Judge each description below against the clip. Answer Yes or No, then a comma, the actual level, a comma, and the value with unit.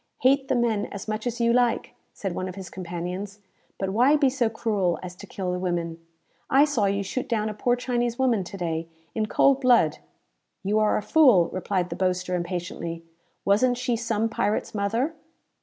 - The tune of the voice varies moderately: Yes, average, 4.9 semitones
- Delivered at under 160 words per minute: No, average, 190 wpm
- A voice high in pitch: Yes, high, 210 Hz